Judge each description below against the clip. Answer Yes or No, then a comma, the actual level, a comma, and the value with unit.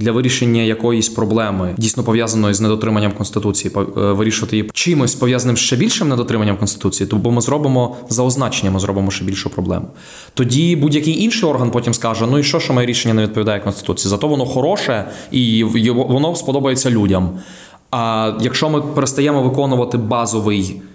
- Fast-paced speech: Yes, fast, 165 wpm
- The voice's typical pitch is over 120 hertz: No, low, 115 Hz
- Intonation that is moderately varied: Yes, average, 3.6 semitones